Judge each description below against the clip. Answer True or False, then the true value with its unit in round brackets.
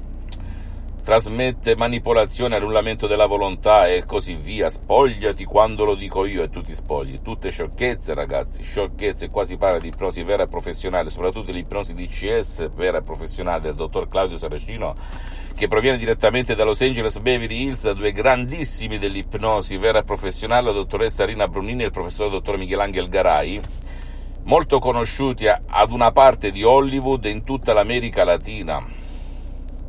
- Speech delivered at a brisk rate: False (155 wpm)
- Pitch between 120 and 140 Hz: False (105 Hz)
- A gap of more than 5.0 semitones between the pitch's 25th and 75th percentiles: True (5.4 semitones)